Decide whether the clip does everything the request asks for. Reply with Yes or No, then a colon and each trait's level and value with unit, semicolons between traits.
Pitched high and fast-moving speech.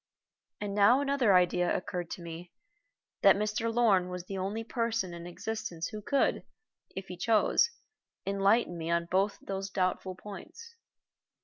No: high, 195 Hz; average, 145 wpm